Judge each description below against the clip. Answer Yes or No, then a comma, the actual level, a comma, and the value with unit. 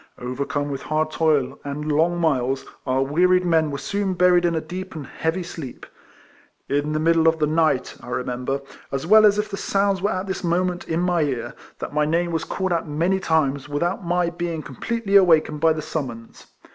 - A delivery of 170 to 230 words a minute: Yes, average, 200 wpm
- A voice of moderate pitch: Yes, medium, 160 Hz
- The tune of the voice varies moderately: Yes, average, 3.6 semitones